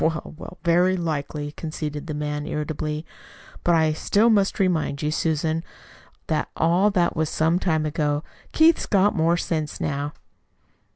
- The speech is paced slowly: No, average, 150 wpm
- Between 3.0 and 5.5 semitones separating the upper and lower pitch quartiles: No, narrow, 2.5 semitones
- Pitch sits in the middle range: Yes, medium, 160 Hz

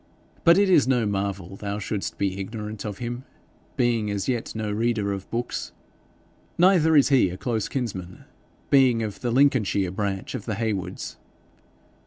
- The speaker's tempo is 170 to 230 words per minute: No, average, 160 wpm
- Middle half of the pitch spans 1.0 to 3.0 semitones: No, average, 3.8 semitones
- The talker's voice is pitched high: No, low, 110 Hz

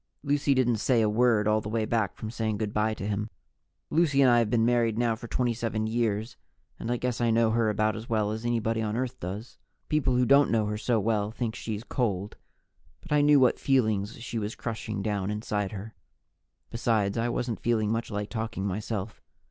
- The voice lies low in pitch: Yes, low, 110 Hz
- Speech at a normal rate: No, fast, 210 wpm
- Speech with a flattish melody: Yes, narrow, 2.1 semitones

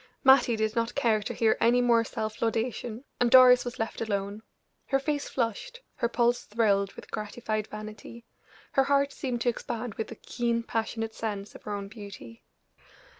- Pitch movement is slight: Yes, narrow, 2.2 semitones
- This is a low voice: No, high, 230 Hz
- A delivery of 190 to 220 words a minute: No, average, 175 wpm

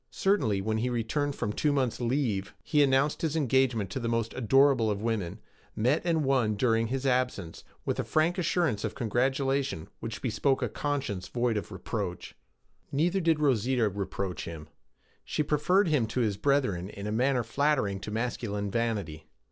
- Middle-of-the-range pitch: No, low, 120 Hz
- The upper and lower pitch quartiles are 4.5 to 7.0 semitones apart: Yes, average, 5.0 semitones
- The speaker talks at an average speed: Yes, average, 170 wpm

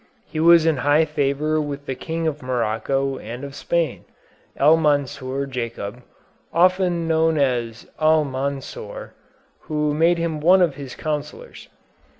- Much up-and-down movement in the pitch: No, average, 3.2 semitones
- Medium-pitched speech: Yes, medium, 150 Hz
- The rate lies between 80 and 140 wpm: Yes, slow, 135 wpm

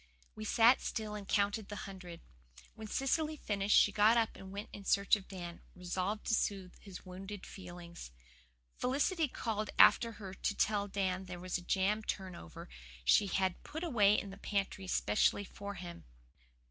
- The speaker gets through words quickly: No, average, 170 wpm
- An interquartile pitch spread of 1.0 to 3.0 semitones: Yes, narrow, 2.5 semitones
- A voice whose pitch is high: Yes, high, 200 Hz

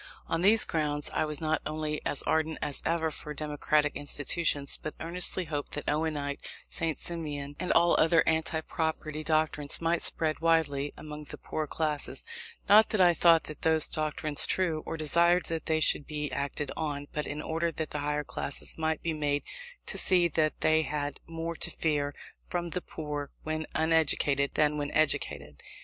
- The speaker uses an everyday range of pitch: No, narrow, 1.8 semitones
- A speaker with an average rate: Yes, average, 175 wpm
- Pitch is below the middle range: No, medium, 155 Hz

